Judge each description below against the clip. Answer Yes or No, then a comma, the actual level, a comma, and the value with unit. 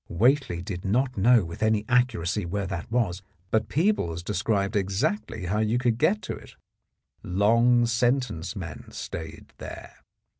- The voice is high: No, low, 105 Hz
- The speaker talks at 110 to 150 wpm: Yes, average, 145 wpm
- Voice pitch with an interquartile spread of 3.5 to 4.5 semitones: No, average, 5.2 semitones